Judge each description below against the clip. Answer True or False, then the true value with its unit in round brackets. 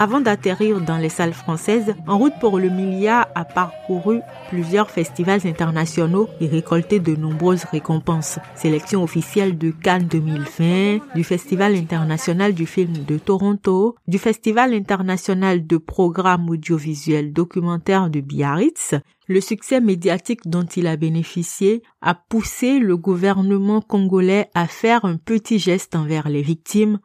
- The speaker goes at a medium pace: False (140 wpm)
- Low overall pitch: False (185 Hz)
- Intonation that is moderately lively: True (3.7 semitones)